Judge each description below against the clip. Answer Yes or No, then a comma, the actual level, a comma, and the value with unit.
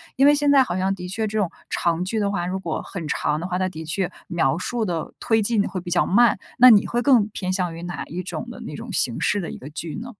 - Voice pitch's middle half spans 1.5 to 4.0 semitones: No, average, 4.4 semitones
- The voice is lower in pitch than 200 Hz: Yes, high, 190 Hz